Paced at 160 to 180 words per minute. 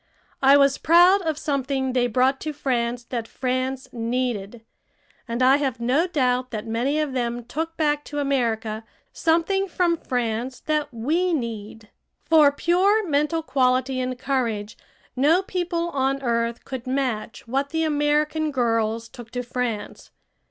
No: average, 145 wpm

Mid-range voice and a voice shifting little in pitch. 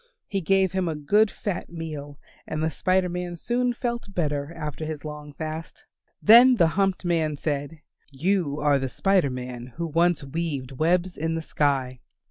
No: medium, 160 Hz; average, 4.1 semitones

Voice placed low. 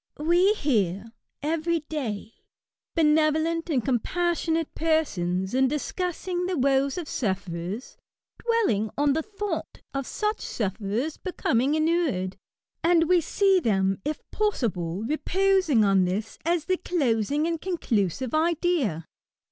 No: very high, 300 Hz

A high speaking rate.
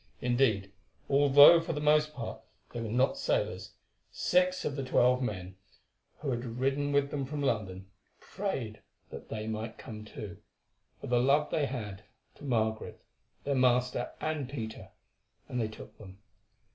No: average, 155 wpm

